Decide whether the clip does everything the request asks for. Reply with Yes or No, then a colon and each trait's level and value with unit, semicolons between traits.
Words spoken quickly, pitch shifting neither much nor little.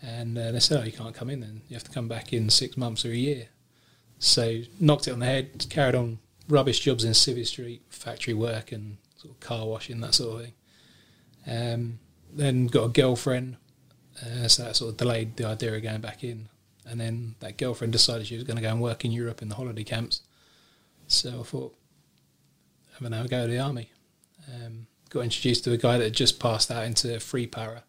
No: fast, 225 wpm; narrow, 1.9 semitones